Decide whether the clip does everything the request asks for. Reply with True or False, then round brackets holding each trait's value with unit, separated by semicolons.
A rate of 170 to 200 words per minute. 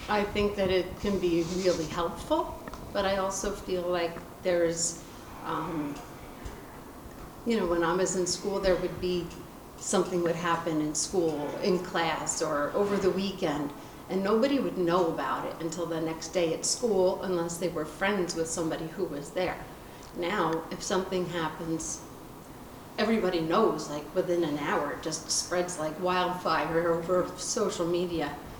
False (155 wpm)